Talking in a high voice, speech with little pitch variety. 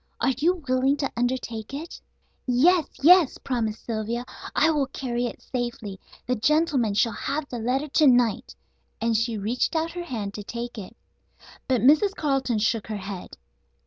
No: high, 245 Hz; average, 4.3 semitones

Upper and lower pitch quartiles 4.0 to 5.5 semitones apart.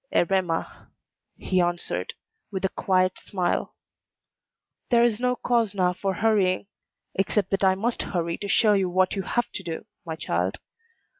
No: average, 2.7 semitones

